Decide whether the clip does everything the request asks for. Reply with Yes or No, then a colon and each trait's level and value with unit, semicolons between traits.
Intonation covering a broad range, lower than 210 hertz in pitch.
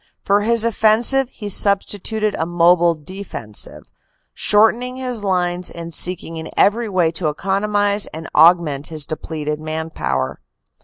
No: average, 4.7 semitones; medium, 185 Hz